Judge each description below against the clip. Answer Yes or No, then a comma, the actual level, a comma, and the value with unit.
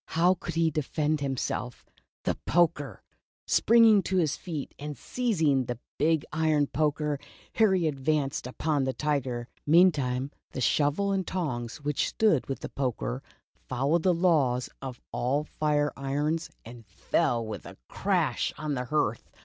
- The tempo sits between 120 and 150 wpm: Yes, average, 145 wpm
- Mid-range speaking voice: Yes, medium, 150 Hz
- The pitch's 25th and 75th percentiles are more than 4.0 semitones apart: No, average, 3.7 semitones